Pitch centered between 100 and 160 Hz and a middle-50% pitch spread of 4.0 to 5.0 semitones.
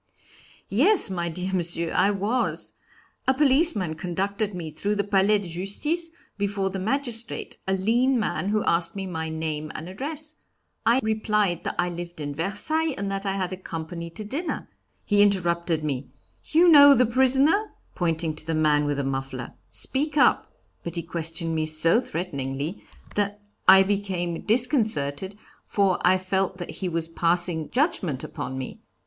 No: high, 190 Hz; average, 4.7 semitones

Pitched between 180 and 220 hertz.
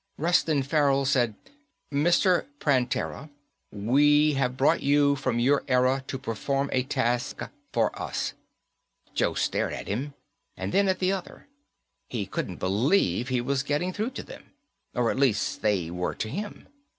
No: low, 135 Hz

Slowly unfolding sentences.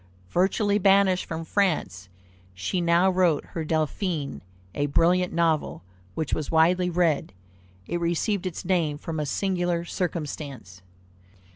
Yes: slow, 125 wpm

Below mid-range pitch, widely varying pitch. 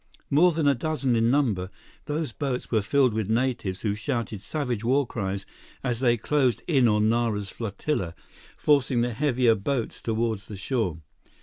No: low, 120 Hz; average, 4.3 semitones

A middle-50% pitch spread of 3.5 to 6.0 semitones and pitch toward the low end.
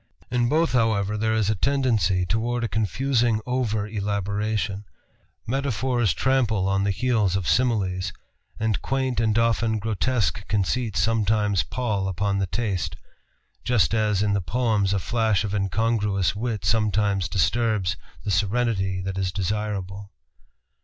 No: average, 2.9 semitones; low, 105 Hz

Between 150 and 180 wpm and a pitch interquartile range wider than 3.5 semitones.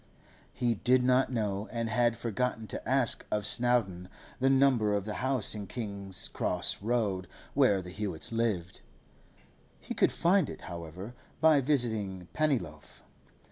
No: average, 140 wpm; average, 4.3 semitones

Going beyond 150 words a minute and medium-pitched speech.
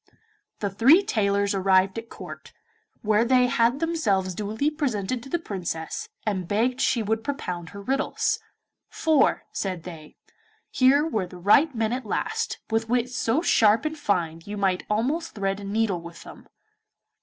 No: average, 165 wpm; high, 220 Hz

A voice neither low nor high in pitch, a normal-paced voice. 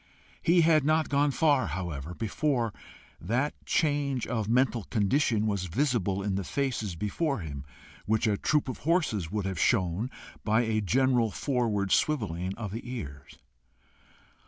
No: low, 115 Hz; average, 145 wpm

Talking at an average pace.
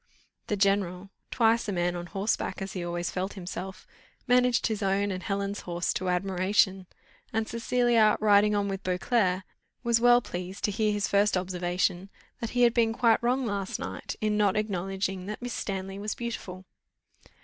Yes: average, 170 wpm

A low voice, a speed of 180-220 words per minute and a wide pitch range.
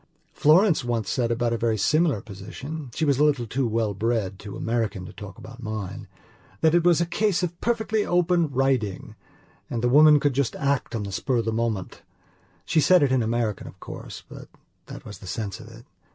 Yes: low, 120 Hz; average, 200 wpm; wide, 5.7 semitones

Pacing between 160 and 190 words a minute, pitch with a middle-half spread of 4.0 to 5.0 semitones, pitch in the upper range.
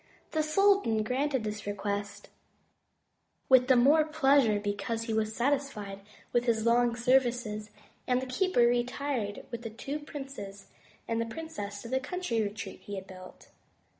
No: average, 150 wpm; average, 4.5 semitones; high, 235 Hz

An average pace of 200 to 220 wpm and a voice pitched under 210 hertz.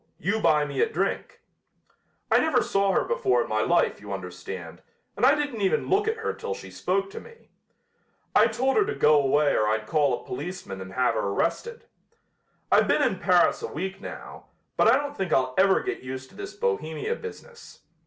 Yes: fast, 205 wpm; high, 190 Hz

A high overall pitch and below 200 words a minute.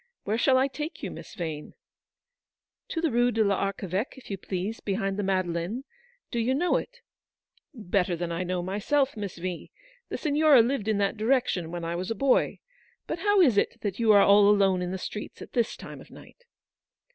No: high, 205 Hz; fast, 205 wpm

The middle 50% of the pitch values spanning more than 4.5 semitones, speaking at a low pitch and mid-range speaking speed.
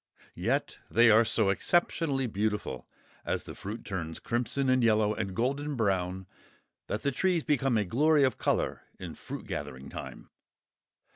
Yes: average, 5.2 semitones; low, 115 Hz; average, 150 wpm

